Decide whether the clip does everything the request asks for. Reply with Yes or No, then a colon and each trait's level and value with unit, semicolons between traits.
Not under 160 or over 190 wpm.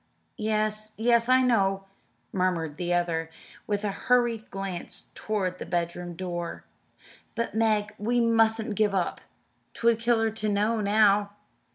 No: average, 140 wpm